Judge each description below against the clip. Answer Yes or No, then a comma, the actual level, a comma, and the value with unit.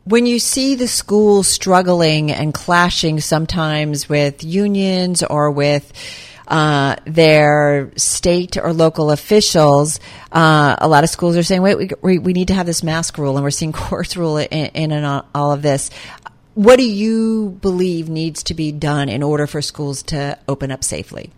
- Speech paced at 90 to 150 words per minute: No, average, 175 wpm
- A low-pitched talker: No, medium, 155 Hz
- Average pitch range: Yes, average, 3.9 semitones